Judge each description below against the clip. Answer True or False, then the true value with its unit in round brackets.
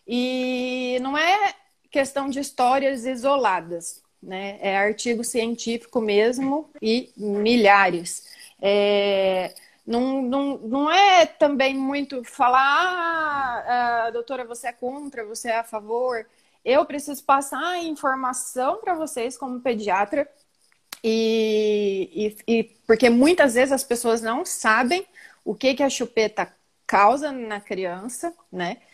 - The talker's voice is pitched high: True (250 Hz)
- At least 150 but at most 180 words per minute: False (120 wpm)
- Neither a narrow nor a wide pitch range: True (3.9 semitones)